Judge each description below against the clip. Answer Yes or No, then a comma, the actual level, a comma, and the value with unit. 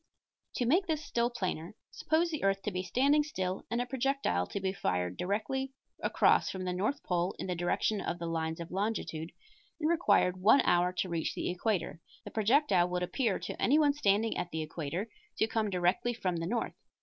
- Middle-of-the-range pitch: No, high, 195 Hz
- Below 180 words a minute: No, average, 195 wpm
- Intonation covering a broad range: Yes, wide, 5.8 semitones